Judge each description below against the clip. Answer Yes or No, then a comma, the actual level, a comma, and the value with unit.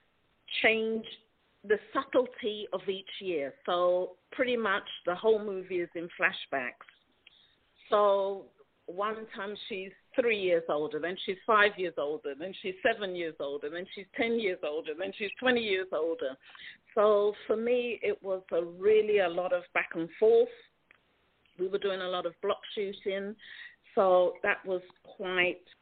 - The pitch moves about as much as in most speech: Yes, average, 3.7 semitones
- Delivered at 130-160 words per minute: Yes, average, 155 wpm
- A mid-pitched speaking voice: No, high, 200 Hz